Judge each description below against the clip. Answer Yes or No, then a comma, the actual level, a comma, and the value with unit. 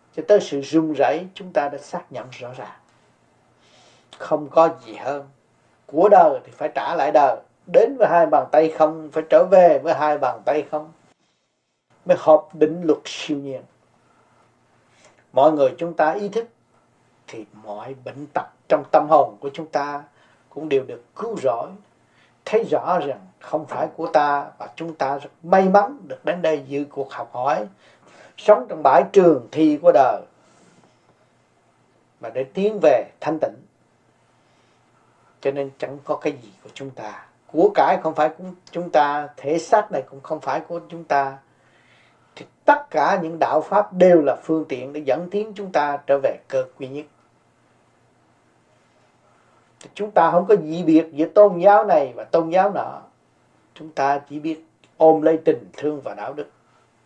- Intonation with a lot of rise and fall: No, average, 3.7 semitones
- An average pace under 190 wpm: Yes, average, 175 wpm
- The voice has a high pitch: No, medium, 155 Hz